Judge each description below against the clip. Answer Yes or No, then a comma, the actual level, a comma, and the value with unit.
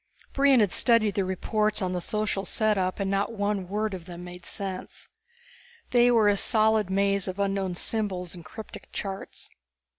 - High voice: Yes, high, 200 Hz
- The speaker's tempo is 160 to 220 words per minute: Yes, average, 170 wpm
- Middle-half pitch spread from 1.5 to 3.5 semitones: Yes, narrow, 2.4 semitones